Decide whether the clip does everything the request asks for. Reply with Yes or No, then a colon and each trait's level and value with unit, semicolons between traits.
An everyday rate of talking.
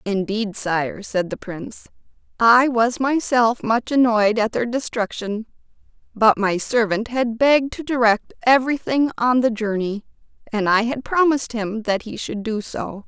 Yes: average, 155 wpm